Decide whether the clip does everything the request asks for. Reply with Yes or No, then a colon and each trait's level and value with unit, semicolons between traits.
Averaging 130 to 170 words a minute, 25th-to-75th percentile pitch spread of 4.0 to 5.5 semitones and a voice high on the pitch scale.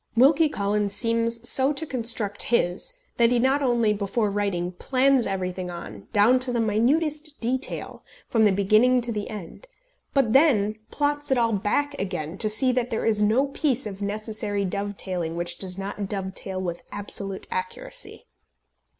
Yes: average, 165 wpm; average, 4.5 semitones; high, 220 Hz